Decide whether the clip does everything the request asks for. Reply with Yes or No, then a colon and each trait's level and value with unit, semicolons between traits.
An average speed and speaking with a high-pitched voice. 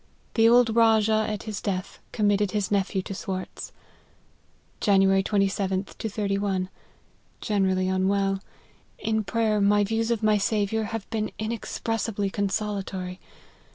No: slow, 130 wpm; high, 205 Hz